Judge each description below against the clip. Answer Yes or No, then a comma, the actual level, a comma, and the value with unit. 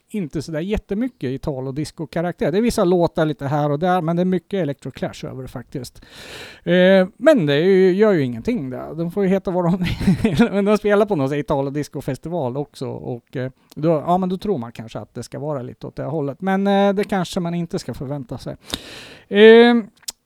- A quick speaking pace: Yes, fast, 210 wpm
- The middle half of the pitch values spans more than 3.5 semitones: Yes, wide, 5.6 semitones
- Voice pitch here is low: No, medium, 170 Hz